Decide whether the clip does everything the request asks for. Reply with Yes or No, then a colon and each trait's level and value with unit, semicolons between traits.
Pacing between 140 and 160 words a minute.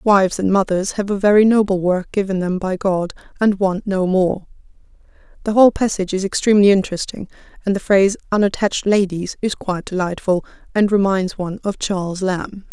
No: average, 170 wpm